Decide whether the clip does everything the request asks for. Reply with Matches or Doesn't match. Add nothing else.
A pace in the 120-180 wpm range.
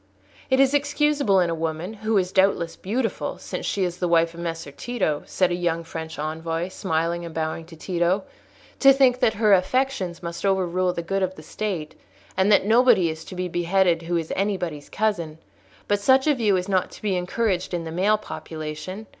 Doesn't match